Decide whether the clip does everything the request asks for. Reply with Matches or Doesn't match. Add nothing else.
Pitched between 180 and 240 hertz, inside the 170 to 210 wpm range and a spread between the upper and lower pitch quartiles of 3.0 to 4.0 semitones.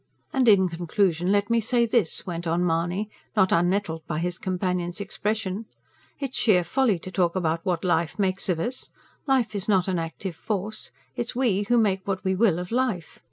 Matches